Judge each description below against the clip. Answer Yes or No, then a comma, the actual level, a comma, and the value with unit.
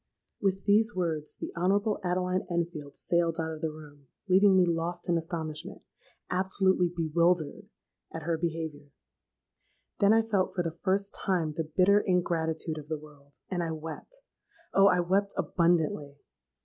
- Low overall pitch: No, medium, 170 Hz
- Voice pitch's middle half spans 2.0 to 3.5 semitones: Yes, average, 2.8 semitones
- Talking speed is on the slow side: No, average, 145 wpm